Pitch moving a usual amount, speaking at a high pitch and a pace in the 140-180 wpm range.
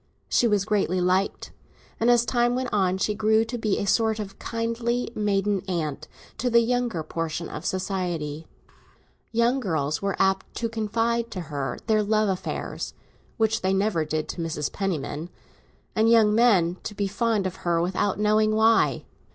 Yes: average, 4.0 semitones; high, 205 Hz; average, 165 wpm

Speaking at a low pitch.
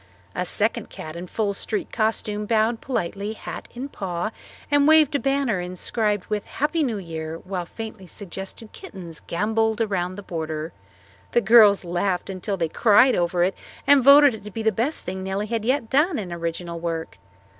No: high, 205 Hz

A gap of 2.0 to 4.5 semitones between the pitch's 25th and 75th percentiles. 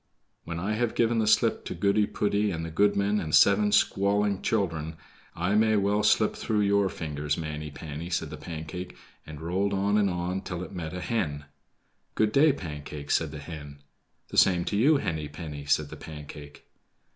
No: average, 5.0 semitones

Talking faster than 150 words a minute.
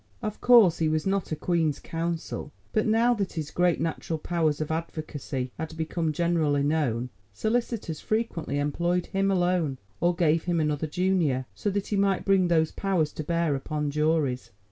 Yes: average, 170 wpm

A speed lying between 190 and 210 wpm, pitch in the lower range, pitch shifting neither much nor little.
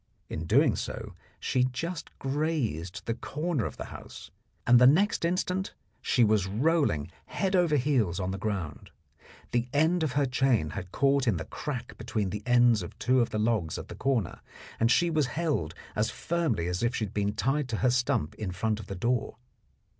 No: average, 195 wpm; low, 120 Hz; wide, 6.3 semitones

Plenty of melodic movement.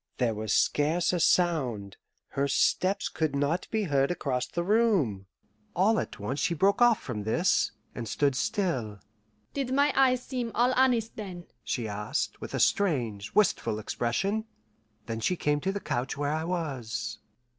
Yes: wide, 8.9 semitones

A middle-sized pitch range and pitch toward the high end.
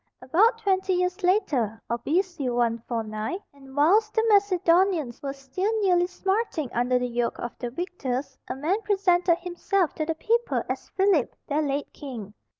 No: wide, 6.9 semitones; very high, 325 Hz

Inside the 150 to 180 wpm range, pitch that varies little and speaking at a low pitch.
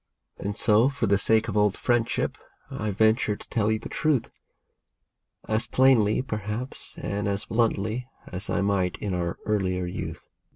Yes: average, 160 wpm; narrow, 2.3 semitones; low, 105 Hz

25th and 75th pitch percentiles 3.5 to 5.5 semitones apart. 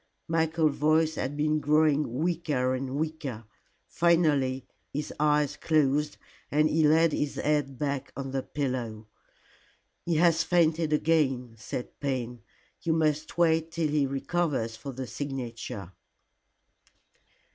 No: average, 3.1 semitones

